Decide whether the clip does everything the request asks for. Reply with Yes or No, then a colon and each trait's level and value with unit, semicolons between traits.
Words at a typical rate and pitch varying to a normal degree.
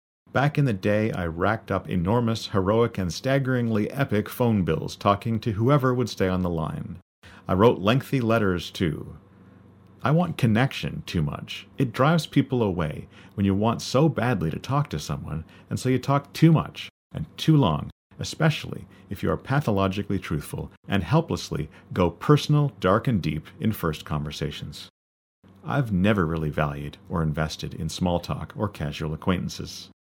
No: average, 165 wpm; wide, 6.3 semitones